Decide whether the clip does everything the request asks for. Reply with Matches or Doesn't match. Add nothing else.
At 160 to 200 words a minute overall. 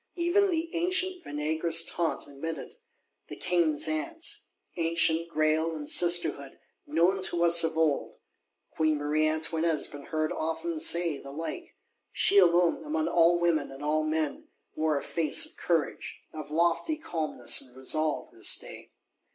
Doesn't match